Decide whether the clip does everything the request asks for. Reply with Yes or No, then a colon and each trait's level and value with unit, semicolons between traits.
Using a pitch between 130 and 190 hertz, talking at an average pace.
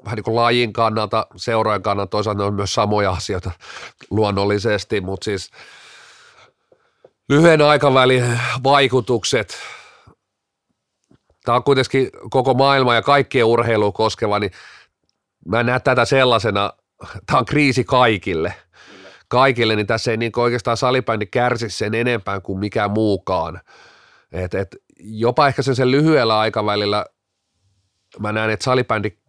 No: low, 115 Hz; average, 115 wpm